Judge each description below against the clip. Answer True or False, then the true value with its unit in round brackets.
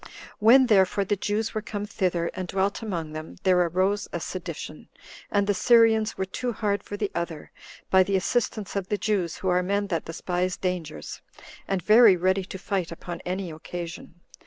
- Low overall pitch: False (190 Hz)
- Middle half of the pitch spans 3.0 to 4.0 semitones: False (2.5 semitones)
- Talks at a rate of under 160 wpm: False (185 wpm)